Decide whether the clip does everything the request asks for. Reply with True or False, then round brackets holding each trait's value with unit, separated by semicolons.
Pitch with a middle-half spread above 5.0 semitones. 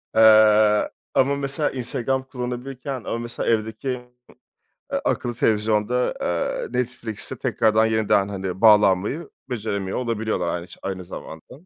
False (3.1 semitones)